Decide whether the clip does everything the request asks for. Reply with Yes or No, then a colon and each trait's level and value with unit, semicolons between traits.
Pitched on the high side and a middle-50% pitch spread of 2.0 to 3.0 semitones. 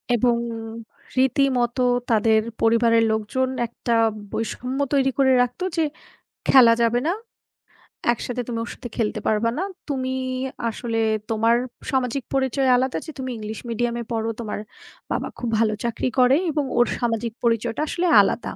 Yes: high, 240 Hz; narrow, 2.4 semitones